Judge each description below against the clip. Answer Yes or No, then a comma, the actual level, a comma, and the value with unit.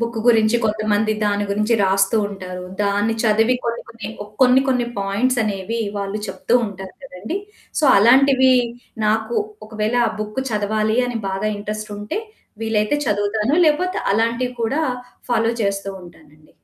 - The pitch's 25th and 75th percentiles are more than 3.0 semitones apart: No, narrow, 2.5 semitones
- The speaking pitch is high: Yes, high, 215 Hz